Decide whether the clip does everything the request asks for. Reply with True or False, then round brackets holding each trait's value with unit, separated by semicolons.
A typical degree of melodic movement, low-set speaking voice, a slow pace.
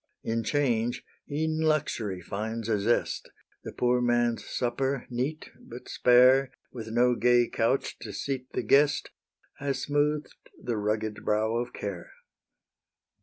True (3.5 semitones; 120 Hz; 130 wpm)